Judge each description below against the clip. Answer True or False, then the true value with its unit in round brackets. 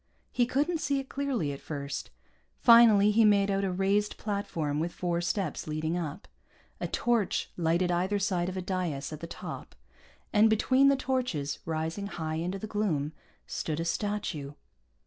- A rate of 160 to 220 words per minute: True (165 wpm)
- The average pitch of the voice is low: False (190 Hz)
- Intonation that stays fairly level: False (4.8 semitones)